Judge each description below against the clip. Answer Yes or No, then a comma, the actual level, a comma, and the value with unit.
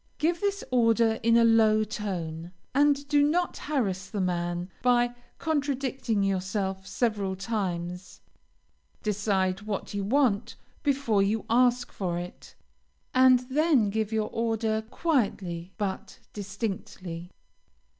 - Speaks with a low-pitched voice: No, high, 215 Hz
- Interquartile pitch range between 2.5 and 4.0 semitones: No, average, 4.8 semitones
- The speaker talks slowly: Yes, slow, 115 wpm